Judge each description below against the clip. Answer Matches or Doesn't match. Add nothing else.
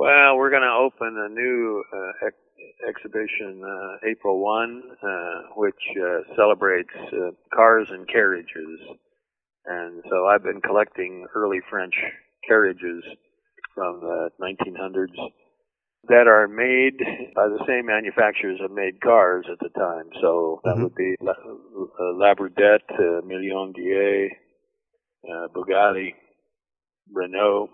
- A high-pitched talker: Doesn't match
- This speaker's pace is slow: Matches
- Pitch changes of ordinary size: Doesn't match